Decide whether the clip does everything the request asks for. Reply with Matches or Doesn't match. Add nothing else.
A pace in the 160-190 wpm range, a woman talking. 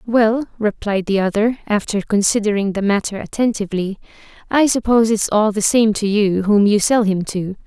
Matches